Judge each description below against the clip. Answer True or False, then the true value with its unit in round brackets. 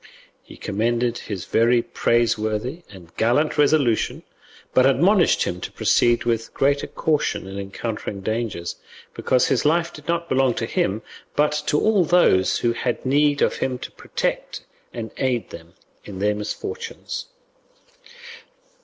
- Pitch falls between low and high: False (120 Hz)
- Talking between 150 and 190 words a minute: False (140 wpm)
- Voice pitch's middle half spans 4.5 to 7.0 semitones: True (5.3 semitones)